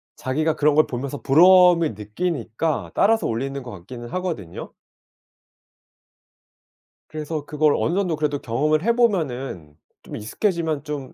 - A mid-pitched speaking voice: Yes, medium, 150 Hz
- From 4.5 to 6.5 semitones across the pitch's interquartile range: Yes, average, 5.1 semitones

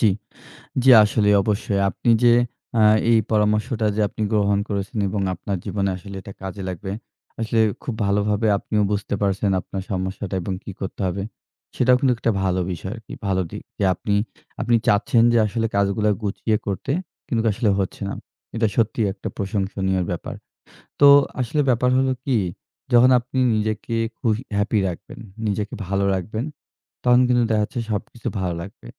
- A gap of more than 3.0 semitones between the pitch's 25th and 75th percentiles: No, average, 2.7 semitones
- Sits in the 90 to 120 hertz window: Yes, low, 105 Hz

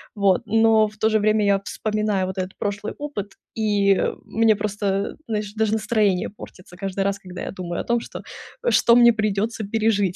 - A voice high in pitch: Yes, high, 210 Hz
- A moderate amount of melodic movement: No, narrow, 1.9 semitones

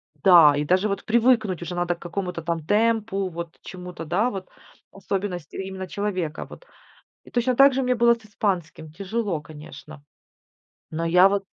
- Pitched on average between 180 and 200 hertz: Yes, medium, 185 Hz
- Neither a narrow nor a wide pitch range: Yes, average, 3.9 semitones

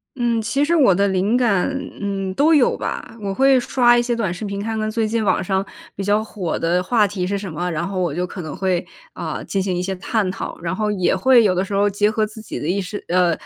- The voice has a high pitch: Yes, high, 200 Hz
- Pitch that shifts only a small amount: No, average, 3.4 semitones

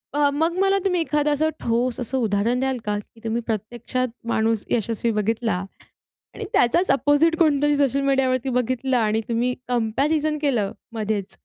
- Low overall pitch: No, very high, 250 Hz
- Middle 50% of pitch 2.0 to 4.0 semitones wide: No, average, 4.4 semitones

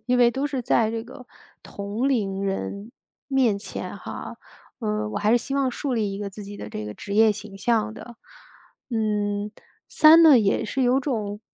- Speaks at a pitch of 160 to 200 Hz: No, high, 220 Hz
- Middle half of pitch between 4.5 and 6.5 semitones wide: No, average, 3.5 semitones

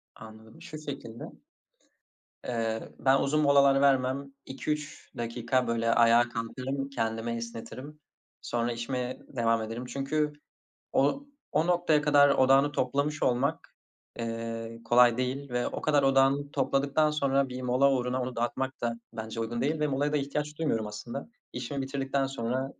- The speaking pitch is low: Yes, low, 130 Hz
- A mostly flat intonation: No, average, 3.2 semitones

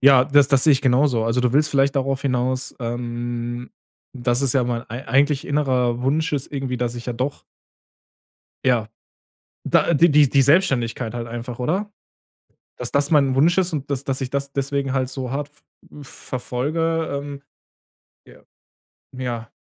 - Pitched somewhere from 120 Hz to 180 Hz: Yes, low, 135 Hz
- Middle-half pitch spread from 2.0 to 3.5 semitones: Yes, narrow, 2.6 semitones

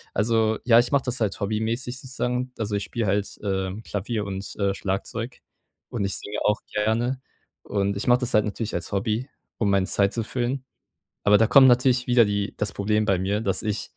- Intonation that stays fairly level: No, average, 3.3 semitones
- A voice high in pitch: No, low, 110 Hz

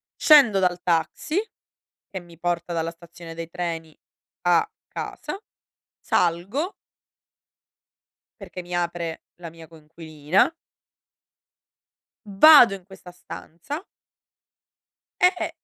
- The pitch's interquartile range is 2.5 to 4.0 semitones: Yes, average, 2.8 semitones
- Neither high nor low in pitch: Yes, medium, 175 Hz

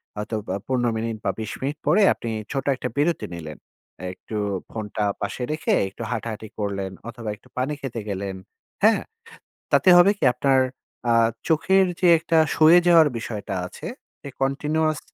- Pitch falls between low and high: No, low, 125 Hz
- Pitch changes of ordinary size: No, wide, 6.5 semitones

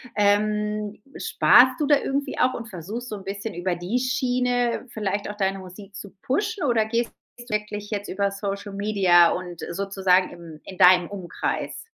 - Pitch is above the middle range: Yes, high, 205 Hz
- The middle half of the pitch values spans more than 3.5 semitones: Yes, average, 3.9 semitones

